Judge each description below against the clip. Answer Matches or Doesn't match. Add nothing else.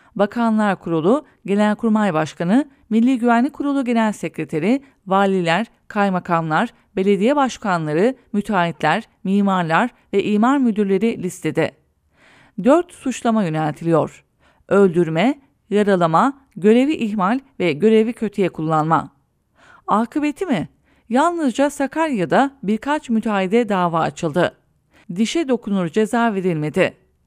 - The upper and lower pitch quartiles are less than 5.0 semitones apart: Doesn't match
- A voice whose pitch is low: Doesn't match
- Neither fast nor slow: Doesn't match